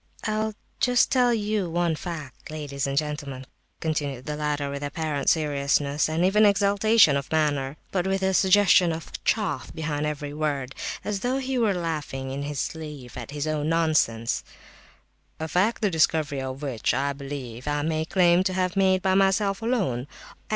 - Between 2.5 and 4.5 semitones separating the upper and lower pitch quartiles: No, average, 5.1 semitones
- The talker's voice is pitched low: No, medium, 155 Hz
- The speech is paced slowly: No, average, 165 wpm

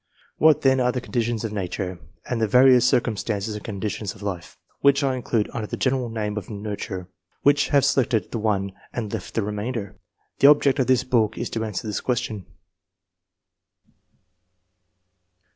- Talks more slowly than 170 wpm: No, average, 175 wpm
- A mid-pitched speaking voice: No, low, 115 Hz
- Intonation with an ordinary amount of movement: Yes, average, 3.6 semitones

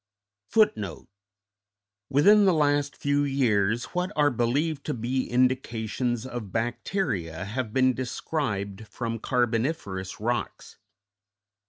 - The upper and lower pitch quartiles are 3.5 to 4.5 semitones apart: No, average, 5.3 semitones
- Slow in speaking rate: Yes, slow, 100 wpm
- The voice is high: No, low, 120 Hz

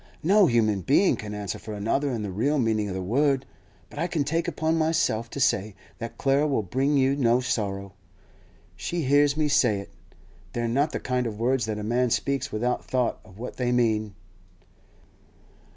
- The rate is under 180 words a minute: No, average, 185 wpm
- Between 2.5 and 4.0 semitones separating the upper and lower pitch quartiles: No, average, 4.8 semitones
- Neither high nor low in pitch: No, low, 125 Hz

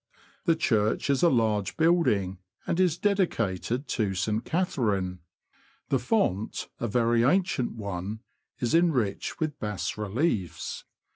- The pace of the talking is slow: Yes, slow, 125 wpm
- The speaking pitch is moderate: No, low, 115 Hz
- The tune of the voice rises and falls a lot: Yes, wide, 8.0 semitones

